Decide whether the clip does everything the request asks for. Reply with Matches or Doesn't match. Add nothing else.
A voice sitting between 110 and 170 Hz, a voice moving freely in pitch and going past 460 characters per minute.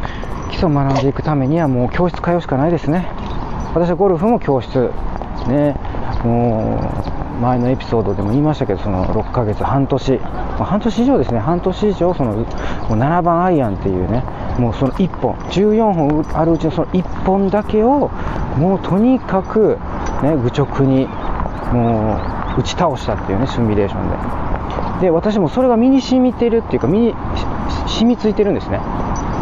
Doesn't match